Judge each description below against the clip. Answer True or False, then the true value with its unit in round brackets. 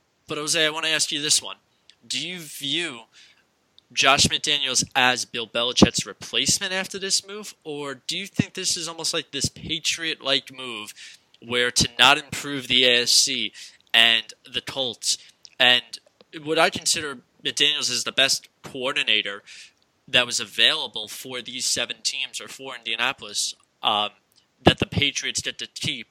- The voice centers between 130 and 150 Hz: True (140 Hz)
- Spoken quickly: False (155 wpm)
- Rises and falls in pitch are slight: False (4.8 semitones)